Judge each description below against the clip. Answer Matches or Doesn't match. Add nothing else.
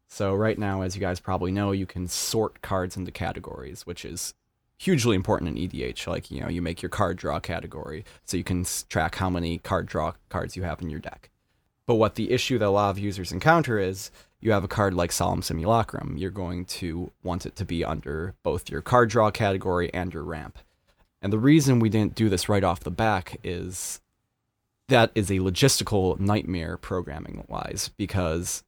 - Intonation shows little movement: Doesn't match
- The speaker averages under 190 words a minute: Doesn't match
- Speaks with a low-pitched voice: Matches